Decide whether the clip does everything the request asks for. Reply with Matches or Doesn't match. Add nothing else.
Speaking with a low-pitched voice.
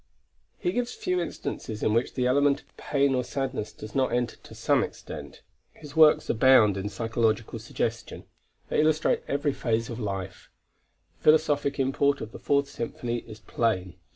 Matches